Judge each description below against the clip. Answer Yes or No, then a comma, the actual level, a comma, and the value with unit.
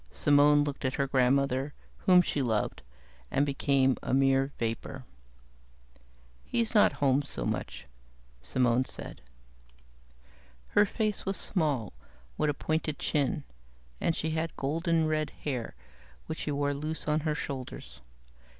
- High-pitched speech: No, medium, 145 Hz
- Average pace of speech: No, slow, 130 wpm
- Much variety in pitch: No, average, 2.9 semitones